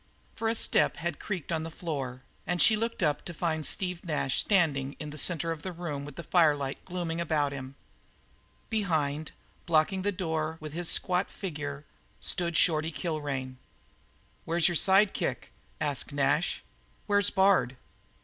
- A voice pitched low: No, medium, 160 Hz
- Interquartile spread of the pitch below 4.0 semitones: Yes, average, 3.5 semitones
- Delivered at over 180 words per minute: No, average, 160 wpm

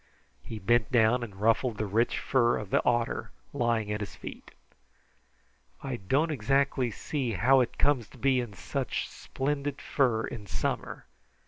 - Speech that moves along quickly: No, average, 155 wpm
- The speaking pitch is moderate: No, low, 120 Hz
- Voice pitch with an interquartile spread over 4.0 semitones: No, average, 3.6 semitones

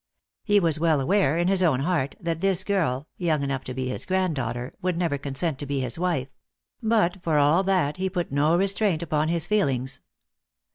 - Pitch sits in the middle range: Yes, medium, 165 Hz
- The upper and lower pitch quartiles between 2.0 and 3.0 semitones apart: No, average, 4.8 semitones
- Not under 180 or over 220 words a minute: Yes, average, 195 wpm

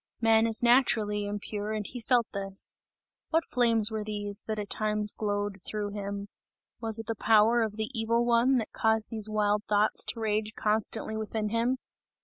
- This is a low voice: No, high, 215 Hz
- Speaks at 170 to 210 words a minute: Yes, average, 175 wpm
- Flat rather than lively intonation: Yes, narrow, 1.5 semitones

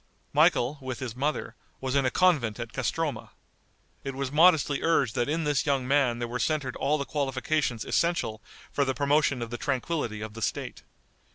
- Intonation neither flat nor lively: Yes, average, 3.5 semitones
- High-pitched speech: No, low, 135 Hz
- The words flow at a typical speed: Yes, average, 185 wpm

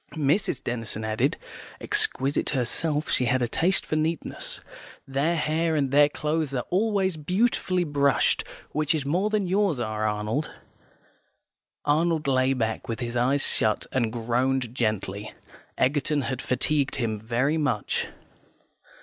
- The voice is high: No, medium, 140 Hz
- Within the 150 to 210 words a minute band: No, slow, 135 wpm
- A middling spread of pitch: Yes, average, 4.7 semitones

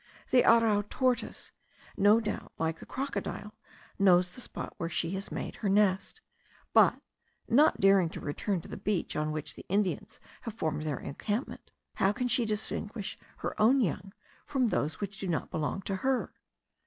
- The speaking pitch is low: No, high, 200 Hz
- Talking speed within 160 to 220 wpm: Yes, average, 170 wpm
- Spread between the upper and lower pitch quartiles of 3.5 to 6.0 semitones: Yes, average, 4.4 semitones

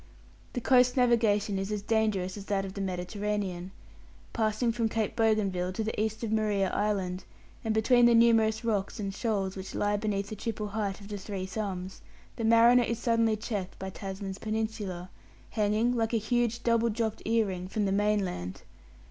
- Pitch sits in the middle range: No, high, 210 Hz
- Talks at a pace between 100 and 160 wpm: No, average, 180 wpm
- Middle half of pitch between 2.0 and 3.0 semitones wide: Yes, narrow, 2.5 semitones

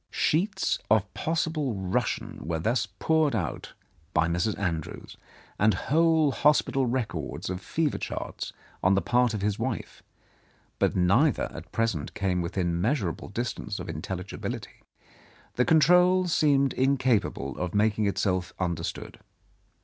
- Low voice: Yes, low, 110 Hz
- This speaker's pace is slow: Yes, slow, 130 wpm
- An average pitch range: No, wide, 7.5 semitones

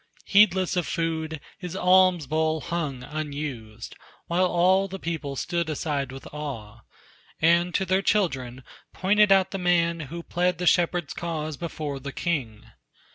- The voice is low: No, medium, 165 Hz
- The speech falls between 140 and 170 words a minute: Yes, average, 145 wpm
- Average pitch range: Yes, average, 3.8 semitones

